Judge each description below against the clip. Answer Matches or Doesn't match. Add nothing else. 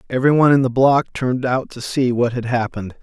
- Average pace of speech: Doesn't match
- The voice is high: Doesn't match